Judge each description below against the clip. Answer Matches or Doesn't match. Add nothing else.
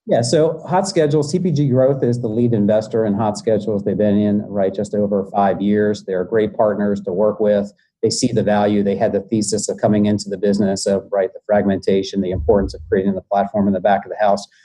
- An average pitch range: Doesn't match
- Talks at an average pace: Doesn't match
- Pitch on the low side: Matches